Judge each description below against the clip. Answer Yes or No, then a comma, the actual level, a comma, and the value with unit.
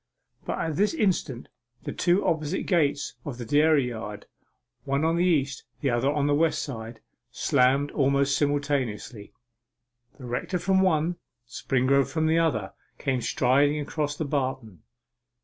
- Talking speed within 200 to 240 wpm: No, average, 150 wpm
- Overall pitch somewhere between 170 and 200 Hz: No, medium, 140 Hz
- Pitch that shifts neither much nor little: Yes, average, 3.7 semitones